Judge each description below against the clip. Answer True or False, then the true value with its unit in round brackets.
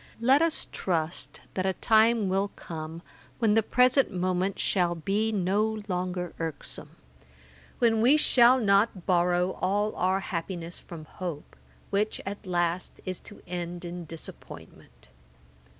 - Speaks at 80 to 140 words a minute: True (135 wpm)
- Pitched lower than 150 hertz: False (185 Hz)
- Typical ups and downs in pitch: True (3.7 semitones)